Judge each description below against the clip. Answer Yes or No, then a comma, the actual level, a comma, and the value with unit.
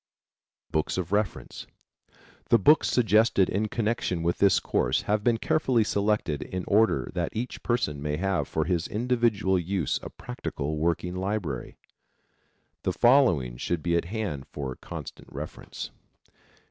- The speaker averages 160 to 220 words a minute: No, average, 140 wpm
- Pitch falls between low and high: No, very low, 95 Hz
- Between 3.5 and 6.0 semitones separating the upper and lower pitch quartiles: Yes, average, 4.9 semitones